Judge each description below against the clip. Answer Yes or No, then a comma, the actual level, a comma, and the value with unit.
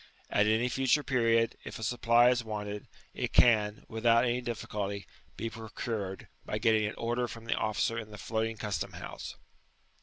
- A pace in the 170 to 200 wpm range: Yes, average, 175 wpm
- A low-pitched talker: Yes, low, 115 Hz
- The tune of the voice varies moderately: No, narrow, 1.9 semitones